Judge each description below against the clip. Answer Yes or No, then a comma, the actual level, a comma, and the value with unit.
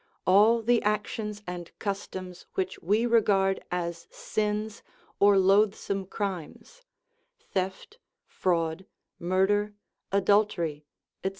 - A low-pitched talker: No, high, 195 Hz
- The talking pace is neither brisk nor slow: No, slow, 95 wpm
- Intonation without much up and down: Yes, narrow, 2.3 semitones